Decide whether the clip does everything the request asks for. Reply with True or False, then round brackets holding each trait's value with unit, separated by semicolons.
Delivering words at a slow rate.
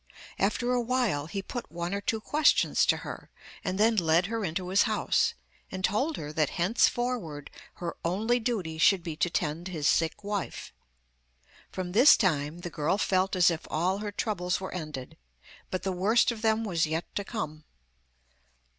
False (175 wpm)